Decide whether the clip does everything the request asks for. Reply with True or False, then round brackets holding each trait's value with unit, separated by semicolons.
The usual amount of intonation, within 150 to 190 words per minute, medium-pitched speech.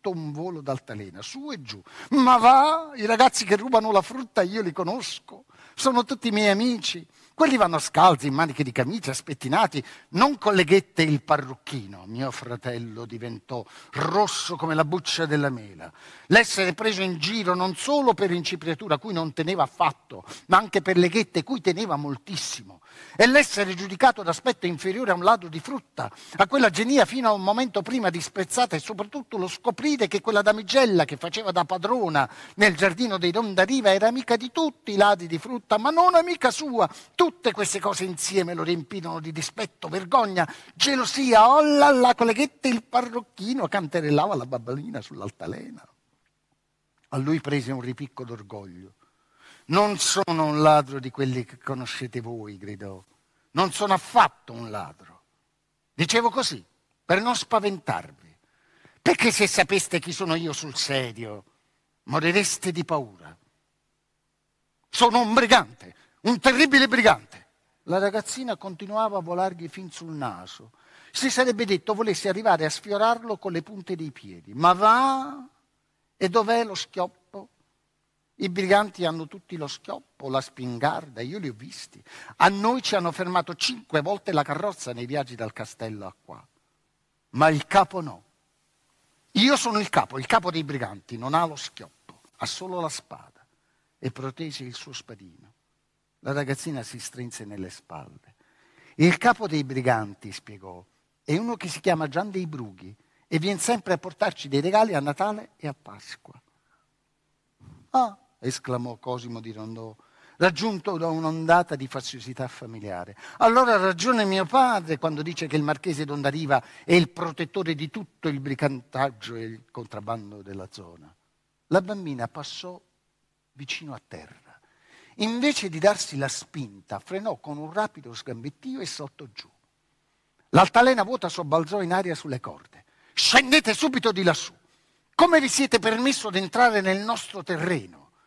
False (7.5 semitones; 155 wpm; 175 Hz)